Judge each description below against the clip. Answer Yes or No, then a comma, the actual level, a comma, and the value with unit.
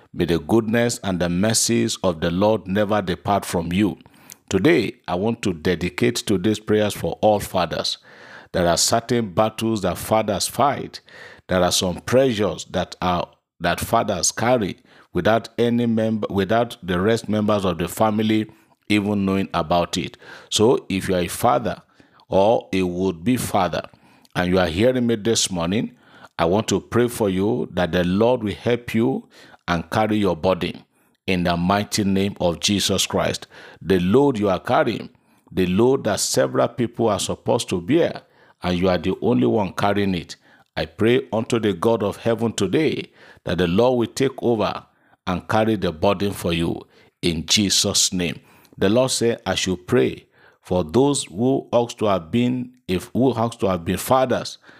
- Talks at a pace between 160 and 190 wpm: Yes, average, 175 wpm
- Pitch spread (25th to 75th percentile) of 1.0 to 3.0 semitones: No, average, 4.0 semitones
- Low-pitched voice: Yes, low, 105 Hz